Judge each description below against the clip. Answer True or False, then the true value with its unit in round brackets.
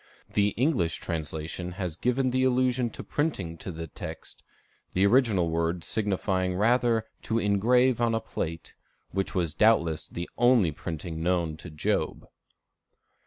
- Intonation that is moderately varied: False (6.3 semitones)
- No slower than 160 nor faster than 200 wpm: False (140 wpm)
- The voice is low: True (95 Hz)